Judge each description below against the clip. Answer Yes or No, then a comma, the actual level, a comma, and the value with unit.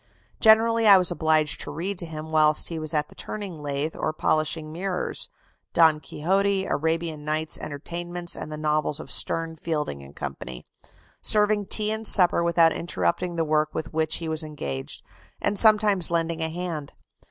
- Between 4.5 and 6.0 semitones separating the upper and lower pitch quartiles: No, average, 2.9 semitones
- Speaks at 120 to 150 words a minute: No, average, 165 wpm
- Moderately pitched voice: Yes, medium, 160 Hz